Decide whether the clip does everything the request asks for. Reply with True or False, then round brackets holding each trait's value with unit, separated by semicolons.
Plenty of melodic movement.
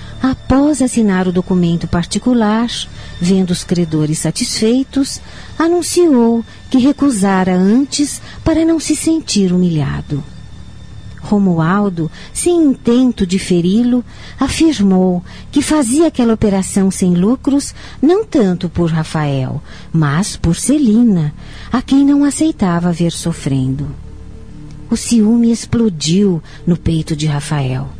True (7.4 semitones)